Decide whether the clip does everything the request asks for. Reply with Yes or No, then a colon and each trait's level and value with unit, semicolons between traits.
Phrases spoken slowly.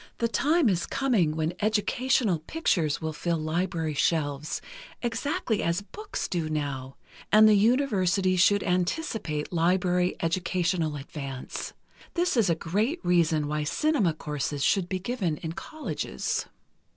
Yes: slow, 130 wpm